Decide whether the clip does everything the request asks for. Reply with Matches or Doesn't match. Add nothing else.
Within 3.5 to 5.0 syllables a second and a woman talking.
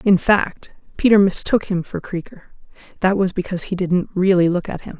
Doesn't match